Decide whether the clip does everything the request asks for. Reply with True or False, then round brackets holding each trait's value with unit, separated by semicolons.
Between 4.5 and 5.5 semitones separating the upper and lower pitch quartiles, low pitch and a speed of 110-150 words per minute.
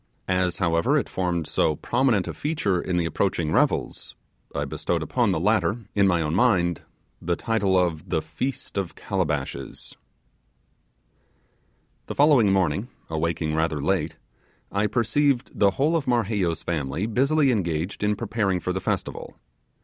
True (5.2 semitones; 95 Hz; 145 wpm)